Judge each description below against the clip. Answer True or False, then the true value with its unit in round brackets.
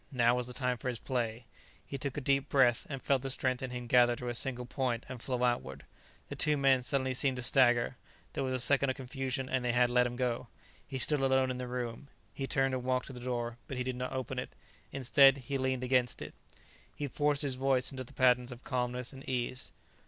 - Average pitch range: False (1.5 semitones)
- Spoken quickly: True (240 wpm)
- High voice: False (130 Hz)